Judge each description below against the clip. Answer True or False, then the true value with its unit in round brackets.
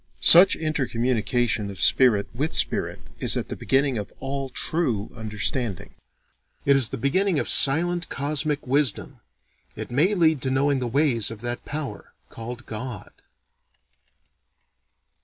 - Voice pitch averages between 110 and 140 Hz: True (135 Hz)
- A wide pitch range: False (4.2 semitones)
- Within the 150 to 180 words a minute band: False (135 wpm)